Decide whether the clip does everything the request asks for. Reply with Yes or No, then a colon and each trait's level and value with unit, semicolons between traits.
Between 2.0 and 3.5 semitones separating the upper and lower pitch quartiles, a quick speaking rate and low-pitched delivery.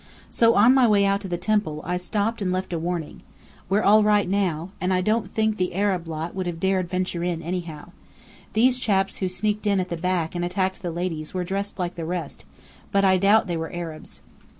No: narrow, 2.6 semitones; fast, 220 wpm; medium, 185 Hz